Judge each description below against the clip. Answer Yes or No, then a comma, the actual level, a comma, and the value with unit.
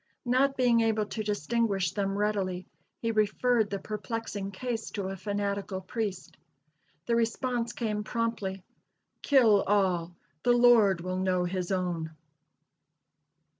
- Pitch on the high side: Yes, high, 205 Hz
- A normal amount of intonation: Yes, average, 3.4 semitones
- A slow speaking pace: Yes, slow, 125 wpm